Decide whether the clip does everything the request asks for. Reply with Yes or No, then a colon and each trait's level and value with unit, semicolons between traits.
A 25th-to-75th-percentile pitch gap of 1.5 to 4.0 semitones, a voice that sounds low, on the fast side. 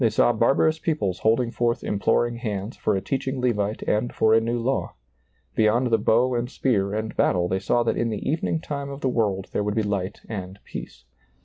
Yes: average, 3.3 semitones; low, 115 Hz; fast, 210 wpm